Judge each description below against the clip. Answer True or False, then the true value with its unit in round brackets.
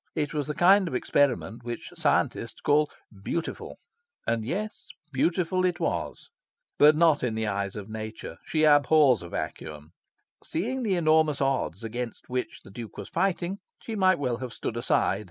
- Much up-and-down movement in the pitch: True (6.6 semitones)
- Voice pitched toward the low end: False (145 Hz)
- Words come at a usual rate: True (165 wpm)